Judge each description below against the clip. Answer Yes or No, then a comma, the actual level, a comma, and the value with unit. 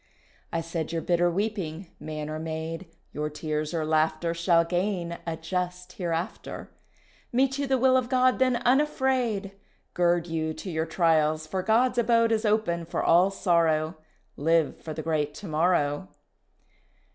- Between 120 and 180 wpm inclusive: Yes, average, 155 wpm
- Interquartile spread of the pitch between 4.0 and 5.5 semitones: Yes, average, 4.9 semitones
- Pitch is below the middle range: No, medium, 170 Hz